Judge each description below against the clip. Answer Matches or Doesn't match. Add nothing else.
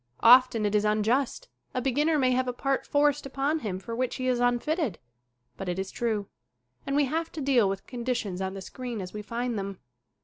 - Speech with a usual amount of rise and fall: Matches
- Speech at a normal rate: Doesn't match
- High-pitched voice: Matches